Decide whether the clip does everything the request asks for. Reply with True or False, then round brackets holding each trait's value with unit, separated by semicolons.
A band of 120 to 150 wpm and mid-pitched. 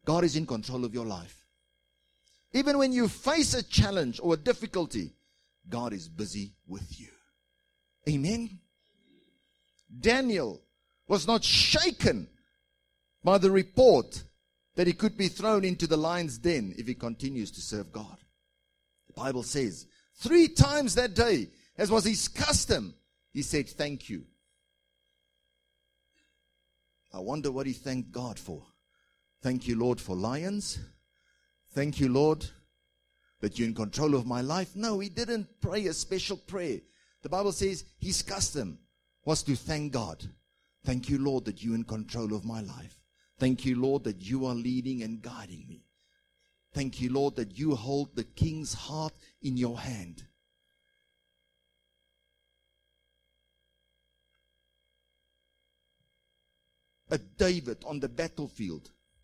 False (135 wpm; 115 Hz)